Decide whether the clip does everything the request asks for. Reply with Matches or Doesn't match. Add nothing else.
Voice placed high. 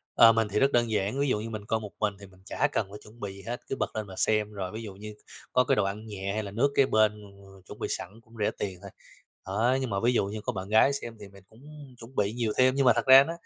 Doesn't match